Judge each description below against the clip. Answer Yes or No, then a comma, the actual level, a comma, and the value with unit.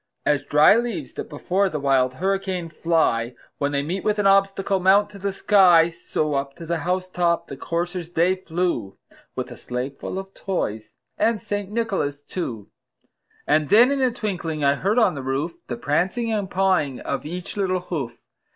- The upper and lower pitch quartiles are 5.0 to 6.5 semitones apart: Yes, average, 5.3 semitones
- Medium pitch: Yes, medium, 175 Hz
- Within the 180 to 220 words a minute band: Yes, average, 185 wpm